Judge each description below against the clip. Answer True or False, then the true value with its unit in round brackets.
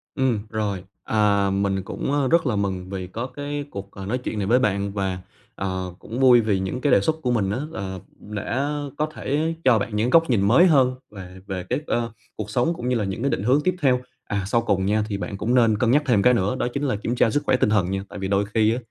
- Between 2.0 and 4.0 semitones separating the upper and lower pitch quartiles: False (4.5 semitones)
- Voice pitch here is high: False (110 Hz)